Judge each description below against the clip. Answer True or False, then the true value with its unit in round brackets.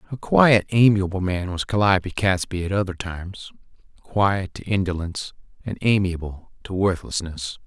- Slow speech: True (125 wpm)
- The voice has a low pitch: True (95 Hz)